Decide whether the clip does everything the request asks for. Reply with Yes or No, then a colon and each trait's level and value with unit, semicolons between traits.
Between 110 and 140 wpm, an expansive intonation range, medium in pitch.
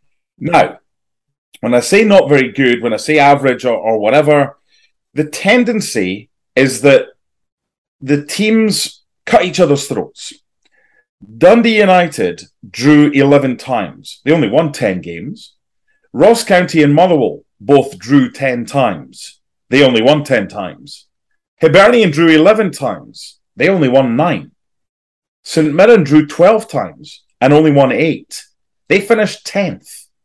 Yes: slow, 135 wpm; wide, 6.8 semitones; medium, 150 Hz